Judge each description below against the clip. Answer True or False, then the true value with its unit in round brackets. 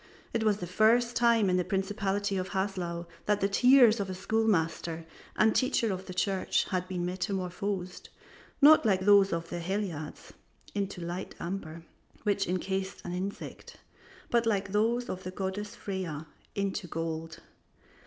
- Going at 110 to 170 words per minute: True (155 wpm)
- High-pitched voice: True (195 Hz)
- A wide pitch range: False (2.5 semitones)